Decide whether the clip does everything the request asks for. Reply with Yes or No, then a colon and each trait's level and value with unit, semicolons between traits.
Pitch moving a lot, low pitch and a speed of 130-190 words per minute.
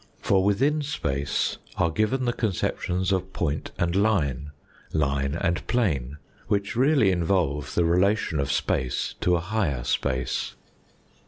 Yes: wide, 6.0 semitones; very low, 90 Hz; slow, 135 wpm